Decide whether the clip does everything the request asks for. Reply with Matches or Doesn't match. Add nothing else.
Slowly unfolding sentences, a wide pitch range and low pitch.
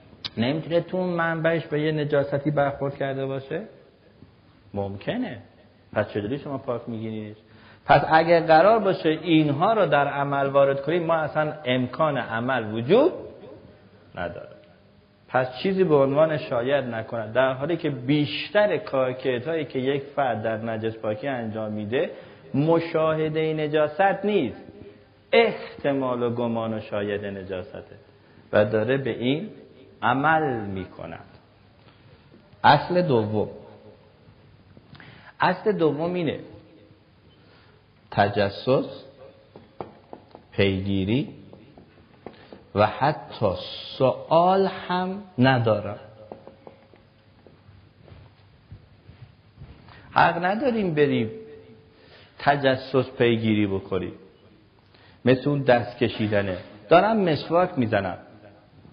Matches